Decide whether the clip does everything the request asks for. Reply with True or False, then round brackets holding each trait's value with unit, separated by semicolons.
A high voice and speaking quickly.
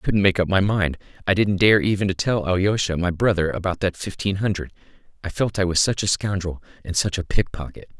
False (95 Hz; 225 wpm)